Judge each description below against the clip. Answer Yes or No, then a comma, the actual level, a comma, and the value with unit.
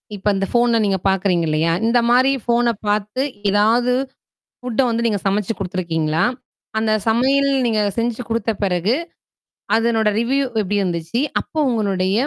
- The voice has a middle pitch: No, high, 215 Hz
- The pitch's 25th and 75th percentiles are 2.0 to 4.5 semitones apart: Yes, average, 3.7 semitones